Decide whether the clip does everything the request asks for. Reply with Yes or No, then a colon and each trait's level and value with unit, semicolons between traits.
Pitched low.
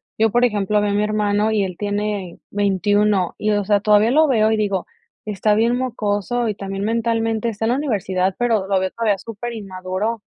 No: high, 210 Hz